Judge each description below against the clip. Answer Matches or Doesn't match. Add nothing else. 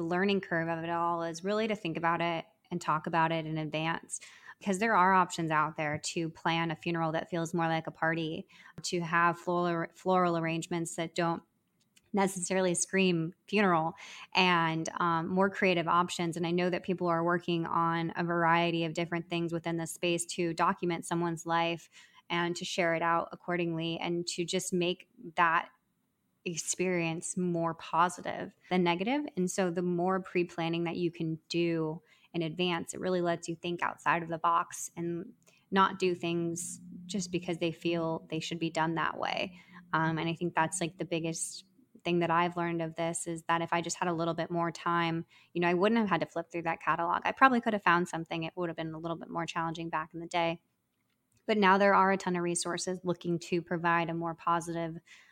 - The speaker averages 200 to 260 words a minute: Matches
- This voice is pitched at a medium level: Matches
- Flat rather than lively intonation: Matches